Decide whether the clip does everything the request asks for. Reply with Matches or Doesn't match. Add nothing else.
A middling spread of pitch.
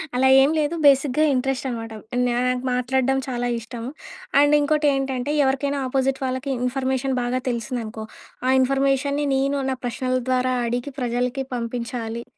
Doesn't match